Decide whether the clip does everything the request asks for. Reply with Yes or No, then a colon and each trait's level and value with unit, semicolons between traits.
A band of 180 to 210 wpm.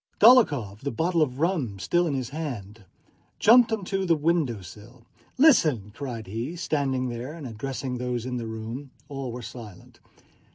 No: average, 160 wpm